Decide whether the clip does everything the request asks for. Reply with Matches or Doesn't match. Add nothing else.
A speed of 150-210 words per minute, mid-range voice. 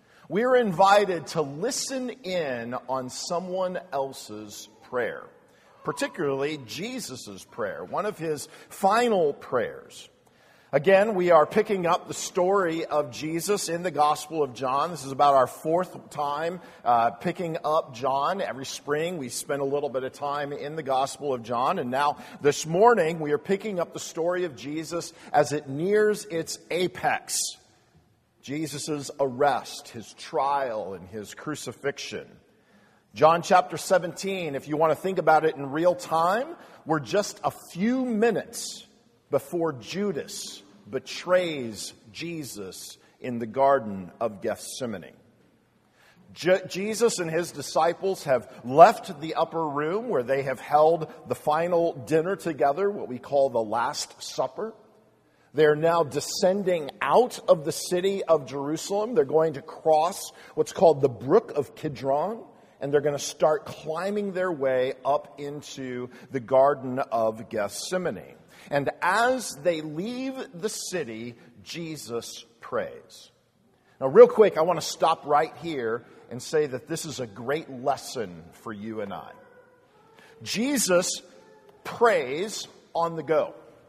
Doesn't match